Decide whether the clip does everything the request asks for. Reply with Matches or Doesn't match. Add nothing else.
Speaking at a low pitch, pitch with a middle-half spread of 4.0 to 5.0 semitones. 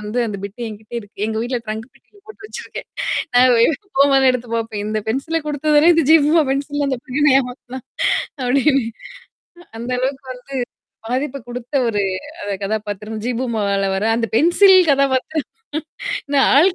Doesn't match